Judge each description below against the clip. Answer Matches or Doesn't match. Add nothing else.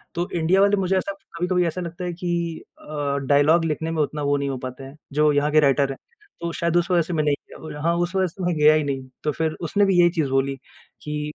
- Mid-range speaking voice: Matches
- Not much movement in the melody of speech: Doesn't match